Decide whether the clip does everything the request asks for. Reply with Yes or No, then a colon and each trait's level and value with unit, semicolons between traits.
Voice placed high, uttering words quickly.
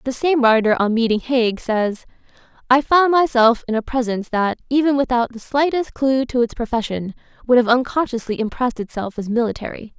No: high, 245 Hz; average, 175 wpm